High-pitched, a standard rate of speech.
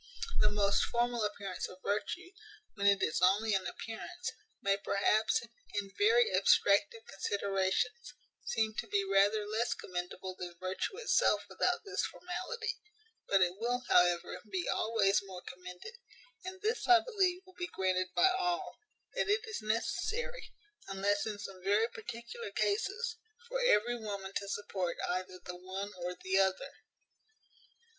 Yes: high, 210 Hz; average, 145 wpm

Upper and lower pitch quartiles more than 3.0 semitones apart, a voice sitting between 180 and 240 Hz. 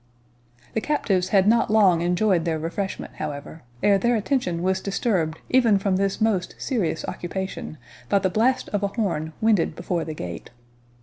Yes: average, 4.2 semitones; high, 190 Hz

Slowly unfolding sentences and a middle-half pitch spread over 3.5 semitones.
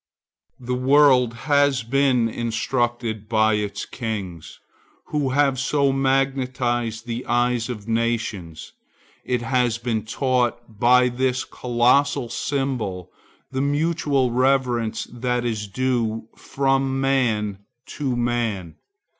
No: slow, 105 wpm; average, 2.8 semitones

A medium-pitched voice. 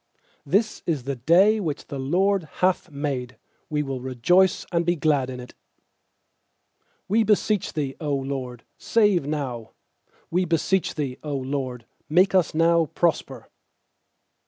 Yes: medium, 155 Hz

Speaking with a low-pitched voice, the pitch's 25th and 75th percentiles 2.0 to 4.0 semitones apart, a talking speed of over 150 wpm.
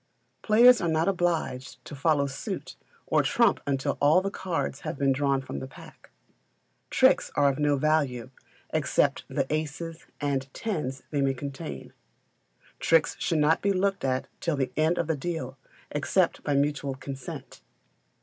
No: medium, 145 Hz; average, 3.4 semitones; average, 160 wpm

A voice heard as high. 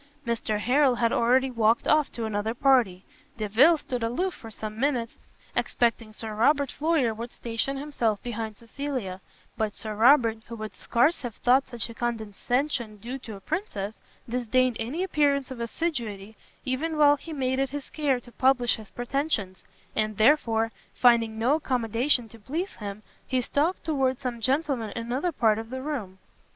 Yes: high, 240 Hz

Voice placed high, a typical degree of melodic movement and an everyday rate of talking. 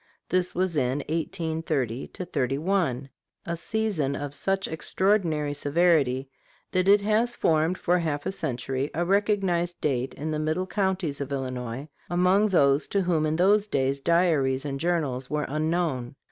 No: medium, 160 Hz; average, 4.7 semitones; average, 145 wpm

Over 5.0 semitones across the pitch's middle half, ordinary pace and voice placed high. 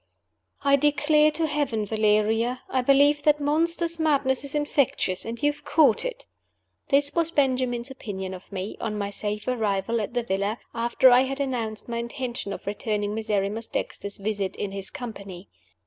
Yes: wide, 5.4 semitones; average, 165 wpm; high, 235 Hz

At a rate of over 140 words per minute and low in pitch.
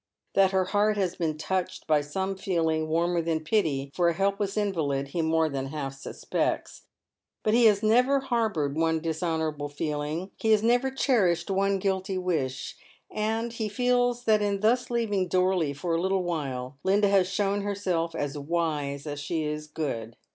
No: average, 170 wpm; medium, 180 Hz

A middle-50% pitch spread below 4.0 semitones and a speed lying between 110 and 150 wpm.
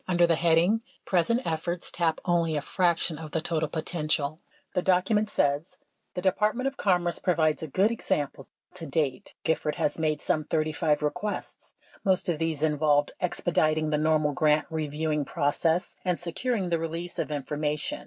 No: average, 2.7 semitones; average, 160 wpm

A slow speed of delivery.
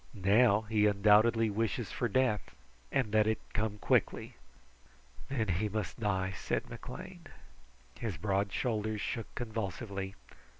Yes: slow, 125 wpm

